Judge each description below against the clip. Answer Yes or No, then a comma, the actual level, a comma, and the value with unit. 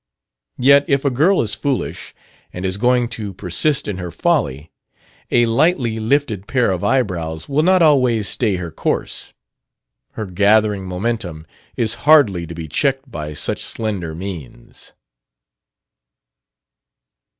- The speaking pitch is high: No, low, 110 Hz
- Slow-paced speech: Yes, slow, 130 wpm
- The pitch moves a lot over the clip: Yes, wide, 6.6 semitones